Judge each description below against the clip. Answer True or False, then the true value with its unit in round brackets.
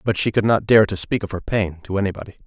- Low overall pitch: True (100 Hz)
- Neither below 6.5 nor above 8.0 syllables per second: True (6.6 syllables/s)